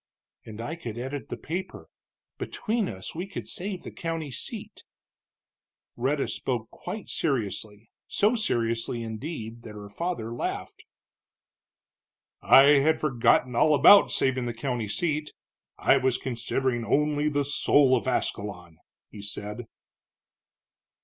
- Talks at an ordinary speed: No, slow, 125 wpm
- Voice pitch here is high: No, low, 130 Hz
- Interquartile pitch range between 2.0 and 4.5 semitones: No, average, 5.0 semitones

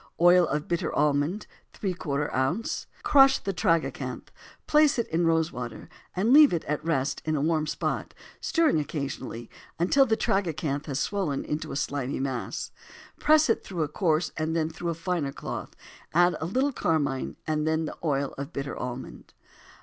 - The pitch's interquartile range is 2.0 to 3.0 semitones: No, average, 4.3 semitones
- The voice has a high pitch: No, medium, 160 Hz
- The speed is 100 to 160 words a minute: No, average, 175 wpm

